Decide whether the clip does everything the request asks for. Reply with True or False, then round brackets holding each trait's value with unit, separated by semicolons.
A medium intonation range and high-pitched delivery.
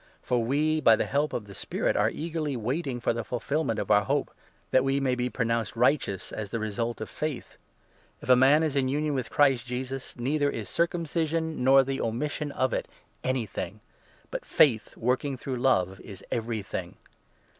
False (4.0 semitones; 130 Hz)